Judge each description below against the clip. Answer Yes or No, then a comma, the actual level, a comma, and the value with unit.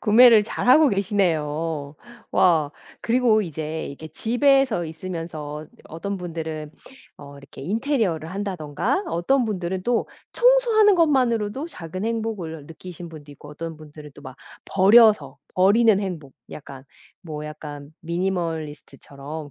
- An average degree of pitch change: No, wide, 6.3 semitones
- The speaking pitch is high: No, medium, 175 Hz